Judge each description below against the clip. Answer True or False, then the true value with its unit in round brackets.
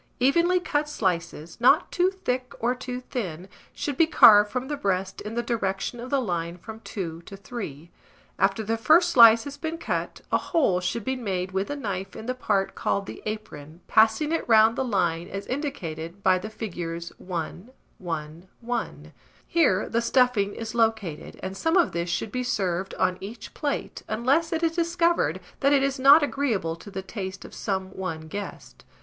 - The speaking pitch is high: True (220 Hz)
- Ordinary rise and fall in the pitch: False (5.8 semitones)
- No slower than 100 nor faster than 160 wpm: False (185 wpm)